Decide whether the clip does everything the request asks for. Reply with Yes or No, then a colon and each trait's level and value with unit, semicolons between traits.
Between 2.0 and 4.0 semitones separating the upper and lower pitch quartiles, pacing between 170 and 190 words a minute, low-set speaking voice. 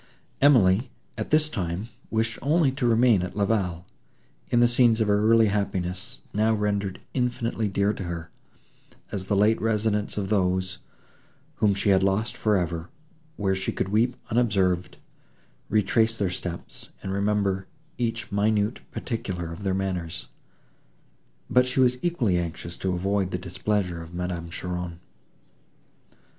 No: average, 3.7 semitones; average, 145 wpm; low, 100 Hz